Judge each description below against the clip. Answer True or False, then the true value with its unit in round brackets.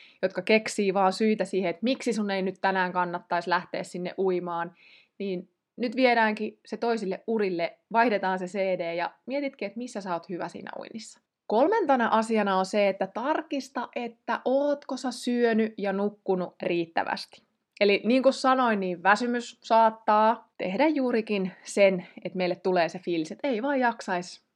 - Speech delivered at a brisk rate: True (160 wpm)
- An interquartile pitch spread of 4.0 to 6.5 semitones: True (4.5 semitones)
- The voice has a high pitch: True (205 Hz)